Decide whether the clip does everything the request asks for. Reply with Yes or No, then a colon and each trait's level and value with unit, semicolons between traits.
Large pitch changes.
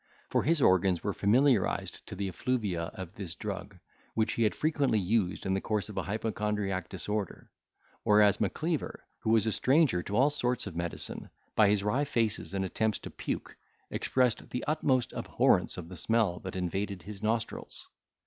No: average, 3.5 semitones